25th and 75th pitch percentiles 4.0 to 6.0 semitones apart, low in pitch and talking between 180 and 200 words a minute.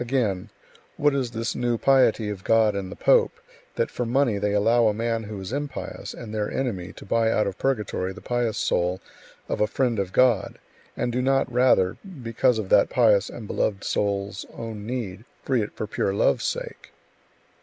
No: average, 3.4 semitones; low, 115 Hz; average, 190 wpm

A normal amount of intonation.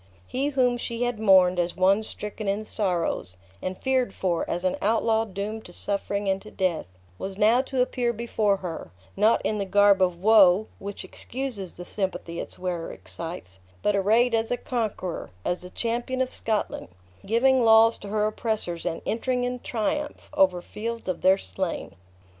Yes: average, 3.8 semitones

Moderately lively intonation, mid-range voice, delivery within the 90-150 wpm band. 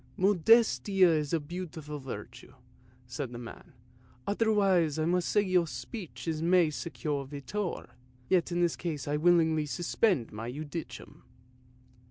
Yes: average, 3.9 semitones; medium, 165 Hz; average, 145 wpm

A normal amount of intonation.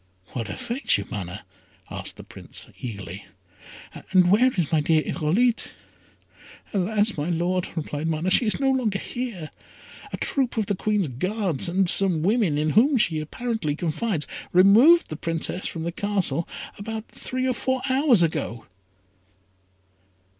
No: wide, 6.3 semitones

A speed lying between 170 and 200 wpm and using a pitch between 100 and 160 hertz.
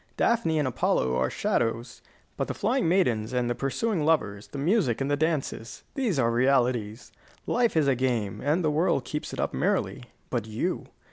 Yes: average, 185 wpm; low, 135 Hz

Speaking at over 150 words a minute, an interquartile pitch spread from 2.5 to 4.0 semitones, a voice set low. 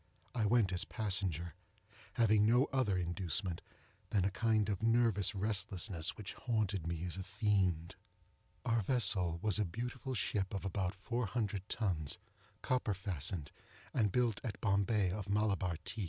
No: average, 145 wpm; average, 3.3 semitones; low, 100 Hz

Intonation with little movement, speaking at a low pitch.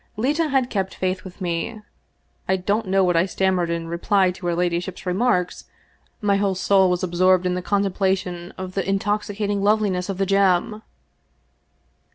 No: narrow, 2.0 semitones; high, 190 Hz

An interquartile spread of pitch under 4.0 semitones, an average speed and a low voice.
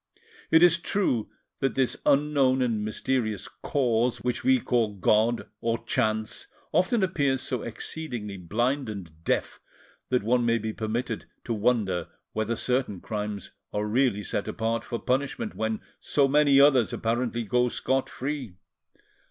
Yes: average, 3.6 semitones; average, 145 wpm; low, 120 Hz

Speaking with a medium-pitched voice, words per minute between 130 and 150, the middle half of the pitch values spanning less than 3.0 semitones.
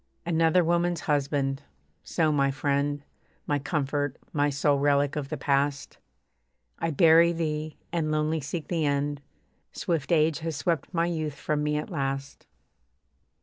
Yes: medium, 150 Hz; average, 145 wpm; narrow, 2.5 semitones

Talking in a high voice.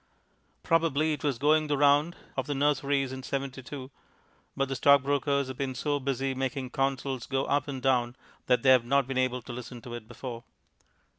No: low, 135 Hz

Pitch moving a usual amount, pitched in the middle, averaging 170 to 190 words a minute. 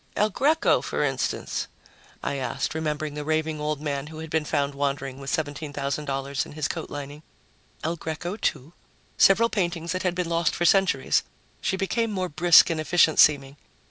Yes: average, 3.3 semitones; medium, 155 Hz; average, 175 wpm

